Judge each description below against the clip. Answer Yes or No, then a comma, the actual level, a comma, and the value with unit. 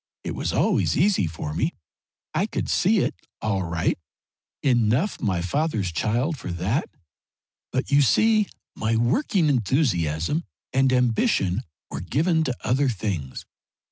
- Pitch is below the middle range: Yes, low, 120 Hz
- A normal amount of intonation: No, wide, 8.1 semitones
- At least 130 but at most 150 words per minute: Yes, slow, 135 wpm